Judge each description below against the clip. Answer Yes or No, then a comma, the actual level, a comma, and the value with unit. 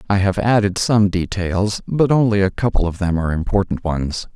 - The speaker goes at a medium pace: Yes, average, 195 wpm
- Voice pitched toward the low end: Yes, low, 100 Hz